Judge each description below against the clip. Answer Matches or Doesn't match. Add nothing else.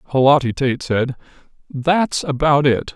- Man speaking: Matches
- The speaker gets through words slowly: Matches